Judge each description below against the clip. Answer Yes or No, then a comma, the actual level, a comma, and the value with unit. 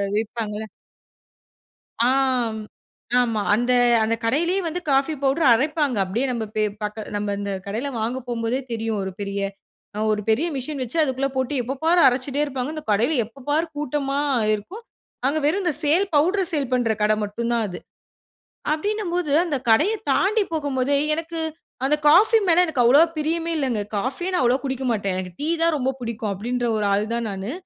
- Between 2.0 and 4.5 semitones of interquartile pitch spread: No, wide, 5.5 semitones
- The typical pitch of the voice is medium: No, very high, 265 Hz